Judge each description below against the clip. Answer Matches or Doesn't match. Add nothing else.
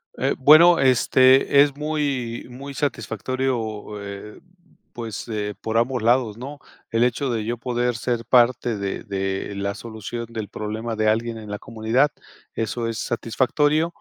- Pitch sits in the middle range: Doesn't match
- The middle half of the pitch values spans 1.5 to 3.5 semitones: Matches